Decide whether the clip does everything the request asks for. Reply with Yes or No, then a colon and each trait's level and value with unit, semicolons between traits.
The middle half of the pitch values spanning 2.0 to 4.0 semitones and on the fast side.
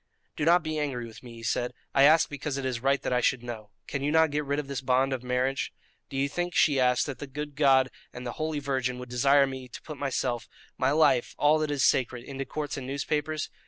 Yes: average, 2.7 semitones; fast, 250 wpm